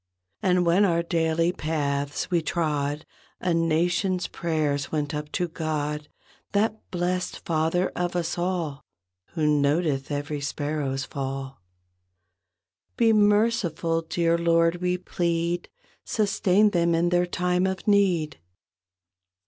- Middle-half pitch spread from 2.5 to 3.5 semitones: Yes, average, 3.0 semitones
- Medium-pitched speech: Yes, medium, 170 Hz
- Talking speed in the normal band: No, slow, 115 wpm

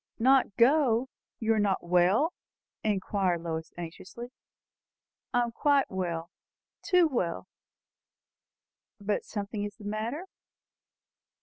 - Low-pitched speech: No, high, 210 Hz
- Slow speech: Yes, slow, 105 wpm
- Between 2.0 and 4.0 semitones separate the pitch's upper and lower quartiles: No, average, 4.8 semitones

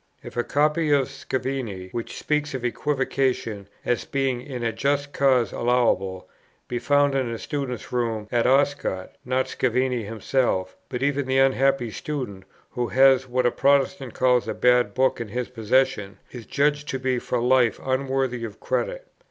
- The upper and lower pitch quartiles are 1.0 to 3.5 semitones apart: Yes, narrow, 2.4 semitones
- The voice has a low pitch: Yes, low, 130 Hz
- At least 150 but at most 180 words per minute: Yes, average, 165 wpm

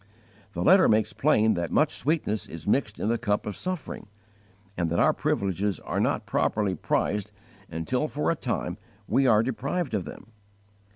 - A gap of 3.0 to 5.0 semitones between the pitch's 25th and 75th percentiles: No, wide, 5.4 semitones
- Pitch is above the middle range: No, low, 110 Hz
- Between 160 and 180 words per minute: Yes, average, 170 wpm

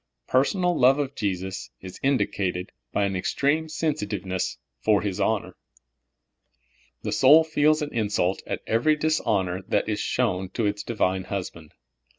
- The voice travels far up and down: Yes, wide, 7.4 semitones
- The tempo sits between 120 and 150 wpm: Yes, average, 145 wpm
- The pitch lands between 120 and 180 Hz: No, low, 105 Hz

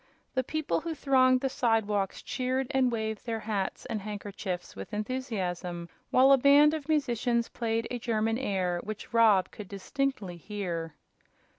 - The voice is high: Yes, high, 225 Hz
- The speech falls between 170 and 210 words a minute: No, average, 150 wpm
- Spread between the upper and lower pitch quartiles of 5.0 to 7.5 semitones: No, average, 4.6 semitones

